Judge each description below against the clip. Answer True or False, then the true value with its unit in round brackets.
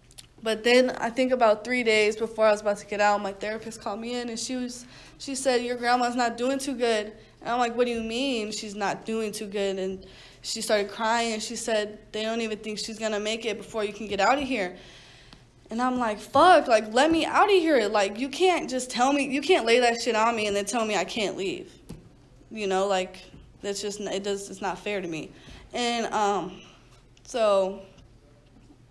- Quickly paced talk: True (225 wpm)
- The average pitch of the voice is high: True (220 Hz)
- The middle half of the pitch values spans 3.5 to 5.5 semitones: False (3.1 semitones)